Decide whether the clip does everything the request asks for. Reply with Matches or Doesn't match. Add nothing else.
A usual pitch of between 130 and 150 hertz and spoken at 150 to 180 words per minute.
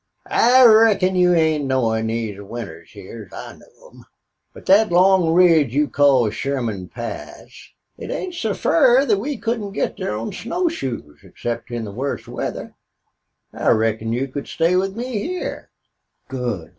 Matches